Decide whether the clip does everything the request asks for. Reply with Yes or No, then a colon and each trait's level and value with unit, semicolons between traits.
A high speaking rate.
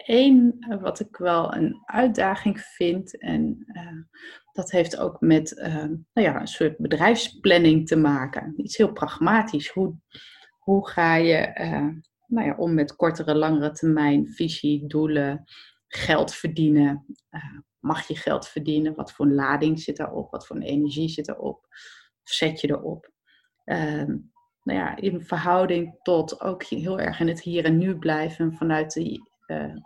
No: average, 155 wpm